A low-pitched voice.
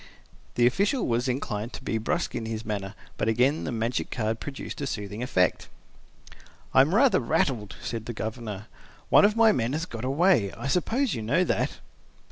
Yes: low, 120 Hz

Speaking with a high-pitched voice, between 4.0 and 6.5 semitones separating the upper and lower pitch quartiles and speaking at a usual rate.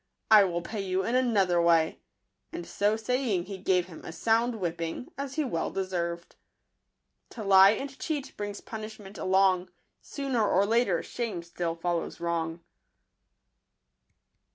Yes: high, 195 Hz; average, 4.5 semitones; average, 145 wpm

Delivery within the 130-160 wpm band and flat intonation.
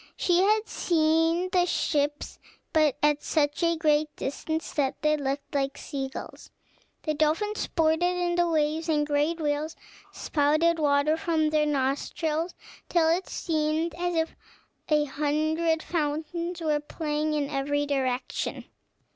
Yes: average, 140 wpm; narrow, 2.3 semitones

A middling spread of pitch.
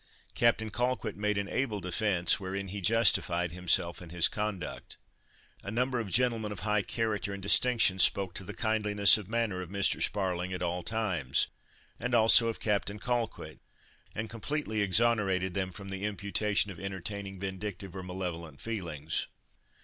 Yes: average, 3.0 semitones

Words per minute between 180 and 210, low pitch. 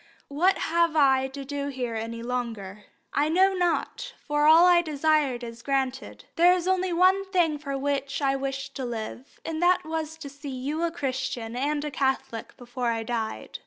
No: average, 185 wpm; very high, 280 Hz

